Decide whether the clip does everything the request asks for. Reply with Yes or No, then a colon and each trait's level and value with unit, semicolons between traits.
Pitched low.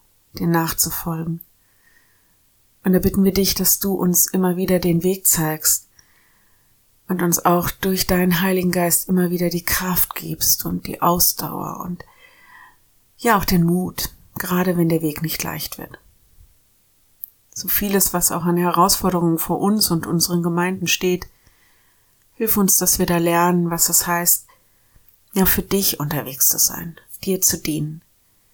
No: medium, 175 Hz